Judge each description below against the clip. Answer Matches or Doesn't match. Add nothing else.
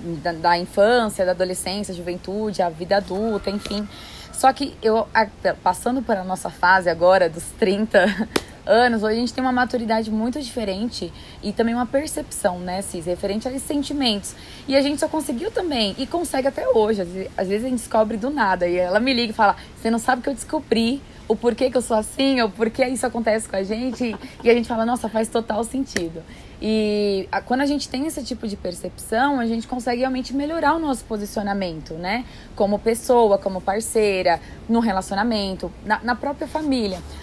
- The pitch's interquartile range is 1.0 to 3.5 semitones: Doesn't match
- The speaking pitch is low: Doesn't match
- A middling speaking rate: Doesn't match